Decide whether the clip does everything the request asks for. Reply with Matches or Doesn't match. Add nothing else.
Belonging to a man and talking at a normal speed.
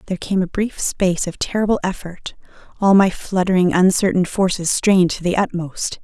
Doesn't match